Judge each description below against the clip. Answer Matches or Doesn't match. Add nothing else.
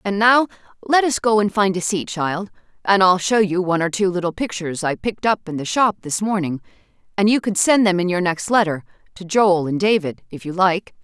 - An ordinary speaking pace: Doesn't match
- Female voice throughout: Matches